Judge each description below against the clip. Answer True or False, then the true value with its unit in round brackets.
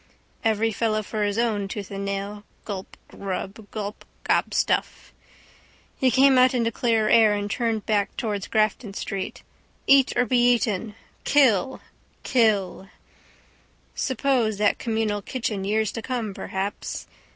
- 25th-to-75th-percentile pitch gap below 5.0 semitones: True (2.6 semitones)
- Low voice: False (215 Hz)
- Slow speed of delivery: True (130 wpm)